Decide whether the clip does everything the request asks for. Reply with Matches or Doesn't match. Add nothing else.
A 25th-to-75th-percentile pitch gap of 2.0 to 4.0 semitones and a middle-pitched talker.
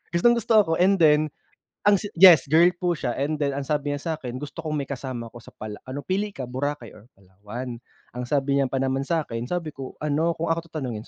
Doesn't match